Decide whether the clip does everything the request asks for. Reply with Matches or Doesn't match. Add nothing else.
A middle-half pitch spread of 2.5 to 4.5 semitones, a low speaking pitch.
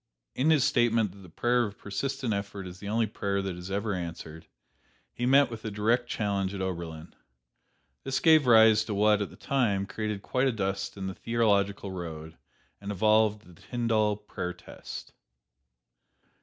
Matches